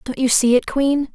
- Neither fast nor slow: No, fast, 260 wpm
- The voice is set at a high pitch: Yes, very high, 260 Hz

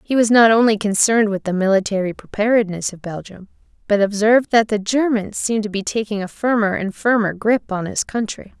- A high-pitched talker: Yes, high, 210 Hz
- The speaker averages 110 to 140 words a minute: No, average, 195 wpm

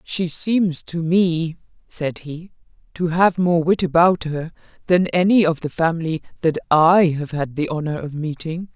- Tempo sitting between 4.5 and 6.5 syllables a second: No, 4.3 syllables/s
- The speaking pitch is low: No, medium, 165 Hz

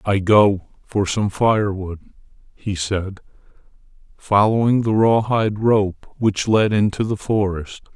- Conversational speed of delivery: No, slow, 130 wpm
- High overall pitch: No, low, 105 Hz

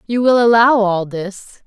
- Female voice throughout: Yes, female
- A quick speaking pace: No, average, 180 wpm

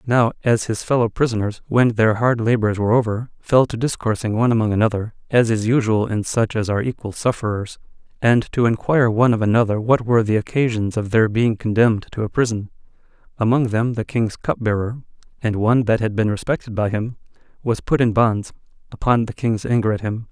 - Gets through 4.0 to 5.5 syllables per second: No, 5.9 syllables/s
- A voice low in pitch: Yes, low, 115 Hz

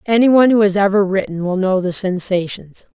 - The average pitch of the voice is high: Yes, high, 195 Hz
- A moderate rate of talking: Yes, average, 185 wpm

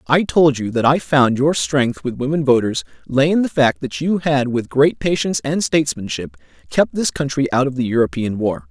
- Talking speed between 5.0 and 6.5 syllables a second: Yes, 5.1 syllables/s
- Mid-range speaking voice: Yes, medium, 145 Hz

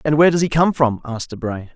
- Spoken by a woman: No, male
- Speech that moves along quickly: Yes, fast, 275 wpm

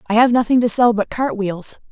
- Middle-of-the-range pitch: No, high, 225 Hz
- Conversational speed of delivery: No, fast, 250 wpm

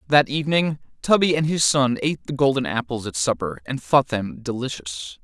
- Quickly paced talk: No, average, 185 wpm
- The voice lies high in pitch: No, low, 135 Hz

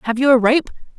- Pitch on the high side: Yes, very high, 250 Hz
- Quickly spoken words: Yes, fast, 245 wpm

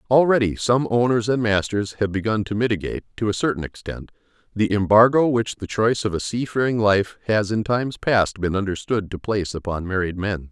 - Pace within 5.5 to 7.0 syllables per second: Yes, 5.6 syllables/s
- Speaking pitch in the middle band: No, low, 105 Hz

